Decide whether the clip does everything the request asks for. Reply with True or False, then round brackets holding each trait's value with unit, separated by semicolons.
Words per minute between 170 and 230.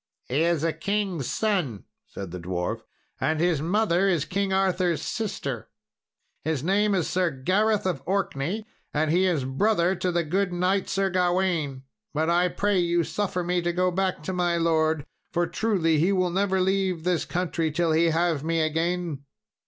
True (175 wpm)